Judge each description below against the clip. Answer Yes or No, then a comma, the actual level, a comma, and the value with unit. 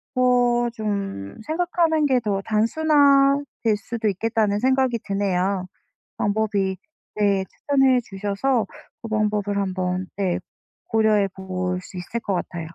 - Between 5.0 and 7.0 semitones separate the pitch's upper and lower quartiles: No, average, 4.3 semitones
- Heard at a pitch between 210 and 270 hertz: Yes, high, 215 Hz